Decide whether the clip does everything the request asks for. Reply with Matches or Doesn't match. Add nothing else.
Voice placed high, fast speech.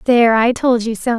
Matches